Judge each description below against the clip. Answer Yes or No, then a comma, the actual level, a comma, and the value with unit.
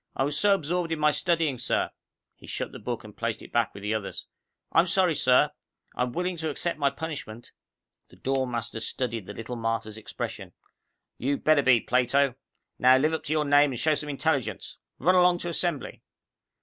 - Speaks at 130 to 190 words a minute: No, average, 200 wpm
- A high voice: No, medium, 140 Hz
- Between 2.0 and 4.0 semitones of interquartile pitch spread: No, average, 4.7 semitones